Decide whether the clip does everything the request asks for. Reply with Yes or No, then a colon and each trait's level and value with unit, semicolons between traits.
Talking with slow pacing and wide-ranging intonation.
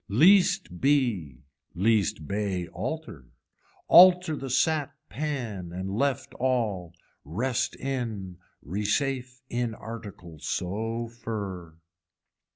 Yes: slow, 90 wpm; wide, 6.3 semitones